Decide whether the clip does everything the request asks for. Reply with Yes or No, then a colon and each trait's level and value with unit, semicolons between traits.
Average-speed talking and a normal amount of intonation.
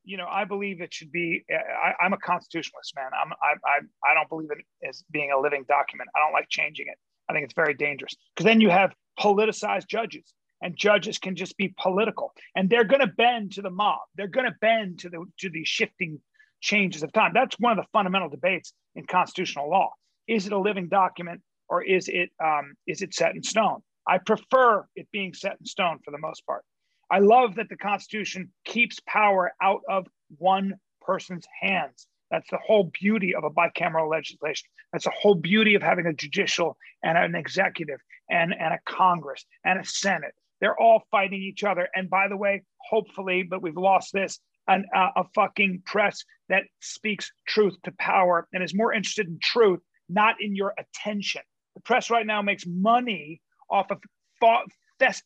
Yes: average, 195 wpm; average, 3.3 semitones